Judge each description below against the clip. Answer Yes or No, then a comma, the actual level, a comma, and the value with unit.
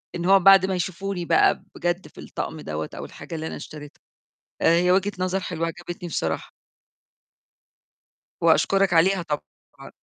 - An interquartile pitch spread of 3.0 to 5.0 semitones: No, narrow, 2.5 semitones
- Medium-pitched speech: Yes, medium, 175 Hz